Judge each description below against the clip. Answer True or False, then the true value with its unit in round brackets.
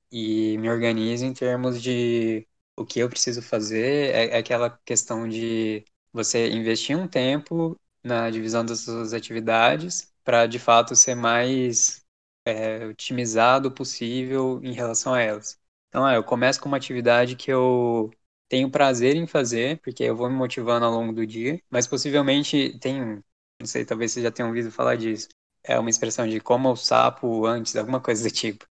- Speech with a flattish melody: True (2.2 semitones)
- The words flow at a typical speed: True (170 wpm)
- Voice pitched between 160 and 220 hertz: False (120 Hz)